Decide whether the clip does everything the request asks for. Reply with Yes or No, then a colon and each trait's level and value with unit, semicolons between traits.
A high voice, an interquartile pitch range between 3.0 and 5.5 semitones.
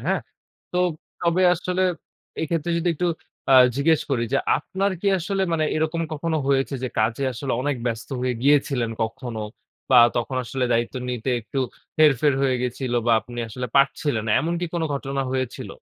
No: low, 135 Hz; average, 4.5 semitones